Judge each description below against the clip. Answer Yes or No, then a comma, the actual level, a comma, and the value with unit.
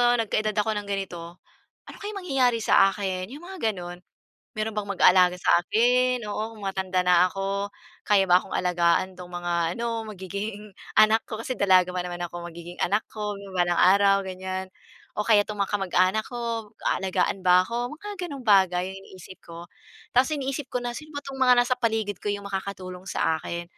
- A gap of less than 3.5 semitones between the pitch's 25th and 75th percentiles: No, average, 4.0 semitones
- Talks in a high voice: Yes, high, 200 Hz